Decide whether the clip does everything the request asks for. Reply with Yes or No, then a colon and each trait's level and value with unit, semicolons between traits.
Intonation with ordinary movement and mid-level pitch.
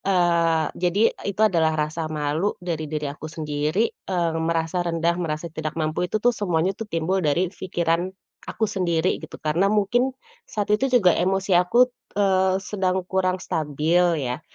Yes: average, 3.1 semitones; medium, 175 Hz